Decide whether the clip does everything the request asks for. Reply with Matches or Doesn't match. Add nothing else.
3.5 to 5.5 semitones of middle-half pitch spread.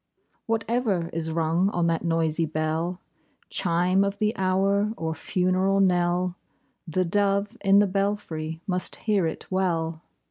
Doesn't match